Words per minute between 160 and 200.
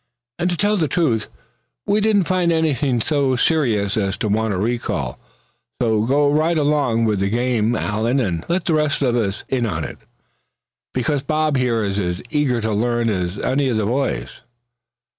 Yes: average, 180 wpm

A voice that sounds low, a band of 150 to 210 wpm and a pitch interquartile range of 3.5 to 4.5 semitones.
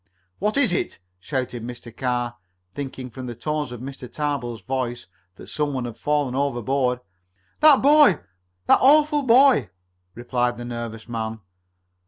No: low, 130 Hz; average, 140 wpm; average, 3.9 semitones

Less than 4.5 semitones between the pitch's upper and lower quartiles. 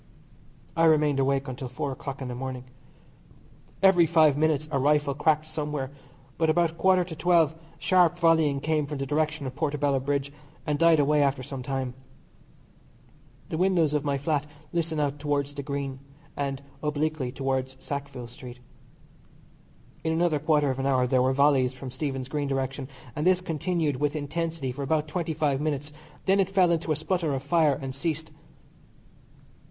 Yes: average, 2.7 semitones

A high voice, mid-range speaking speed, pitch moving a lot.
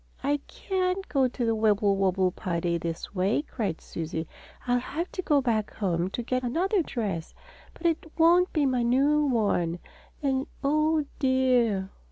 Yes: high, 245 Hz; average, 155 wpm; wide, 7.4 semitones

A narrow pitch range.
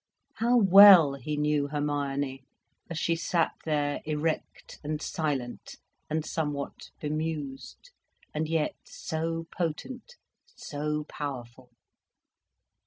Yes: narrow, 2.2 semitones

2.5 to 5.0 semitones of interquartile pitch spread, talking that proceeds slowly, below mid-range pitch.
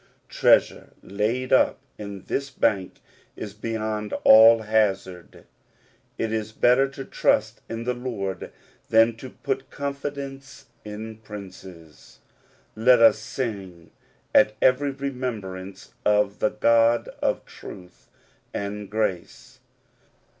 Yes: average, 3.6 semitones; slow, 115 wpm; low, 110 Hz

